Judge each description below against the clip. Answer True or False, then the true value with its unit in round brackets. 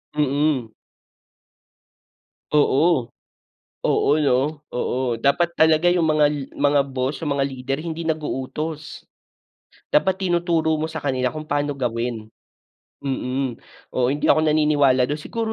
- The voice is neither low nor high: True (145 Hz)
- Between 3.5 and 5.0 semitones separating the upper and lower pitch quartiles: False (3.1 semitones)